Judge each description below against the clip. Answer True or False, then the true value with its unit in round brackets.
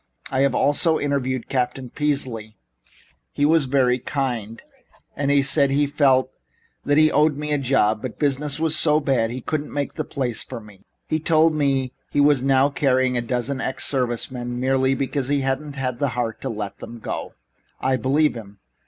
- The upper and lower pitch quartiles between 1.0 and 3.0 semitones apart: True (2.6 semitones)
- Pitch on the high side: False (135 Hz)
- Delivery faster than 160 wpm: True (180 wpm)